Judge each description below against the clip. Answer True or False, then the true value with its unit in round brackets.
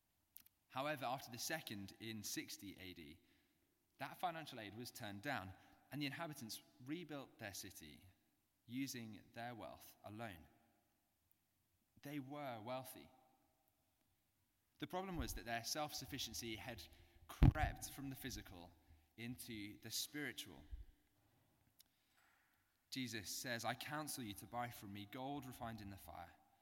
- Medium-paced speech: False (125 wpm)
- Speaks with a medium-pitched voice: False (115 Hz)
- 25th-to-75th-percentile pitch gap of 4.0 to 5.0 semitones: True (4.7 semitones)